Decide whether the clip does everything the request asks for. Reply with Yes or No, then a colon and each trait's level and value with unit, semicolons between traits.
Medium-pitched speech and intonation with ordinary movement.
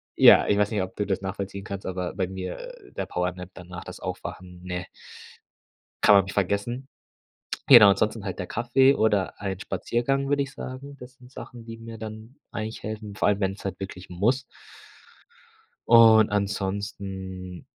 No: low, 100 Hz; average, 3.4 semitones